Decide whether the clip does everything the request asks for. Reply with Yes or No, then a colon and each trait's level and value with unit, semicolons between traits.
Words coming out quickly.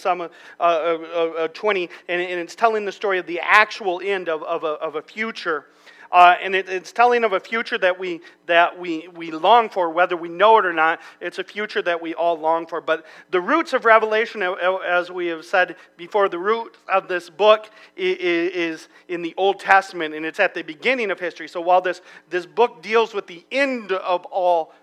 Yes: fast, 220 wpm